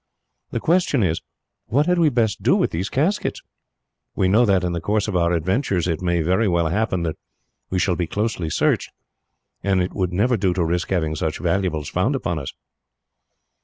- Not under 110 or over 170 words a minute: No, average, 195 wpm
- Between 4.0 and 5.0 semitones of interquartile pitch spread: Yes, average, 4.4 semitones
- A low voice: Yes, very low, 95 Hz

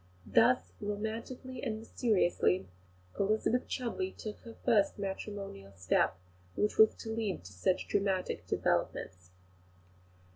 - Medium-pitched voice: No, high, 210 Hz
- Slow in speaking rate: Yes, slow, 110 wpm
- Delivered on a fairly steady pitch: No, average, 4.2 semitones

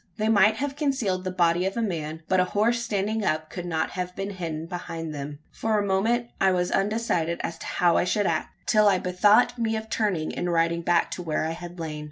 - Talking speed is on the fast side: Yes, fast, 235 wpm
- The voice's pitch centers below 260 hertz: Yes, medium, 185 Hz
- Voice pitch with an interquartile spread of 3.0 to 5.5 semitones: Yes, average, 4.2 semitones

